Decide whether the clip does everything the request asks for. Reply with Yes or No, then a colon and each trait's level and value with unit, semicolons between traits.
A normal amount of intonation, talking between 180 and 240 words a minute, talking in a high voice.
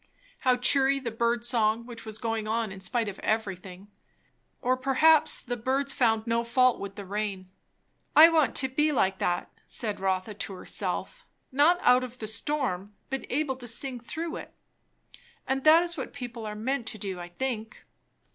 Yes: average, 4.0 semitones; average, 195 wpm; high, 235 Hz